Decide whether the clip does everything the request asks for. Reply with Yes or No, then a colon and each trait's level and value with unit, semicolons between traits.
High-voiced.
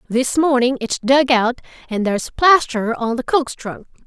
Yes: very high, 255 Hz